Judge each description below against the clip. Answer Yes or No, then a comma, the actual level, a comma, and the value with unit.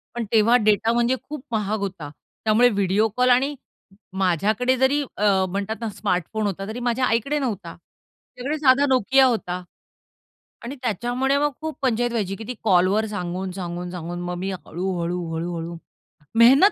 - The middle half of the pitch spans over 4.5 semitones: Yes, average, 5.2 semitones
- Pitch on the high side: Yes, high, 215 Hz